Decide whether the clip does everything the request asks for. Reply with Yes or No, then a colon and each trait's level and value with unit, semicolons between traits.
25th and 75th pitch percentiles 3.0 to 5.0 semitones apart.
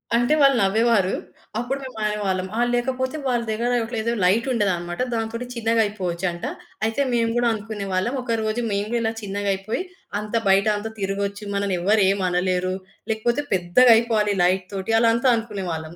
Yes: average, 3.3 semitones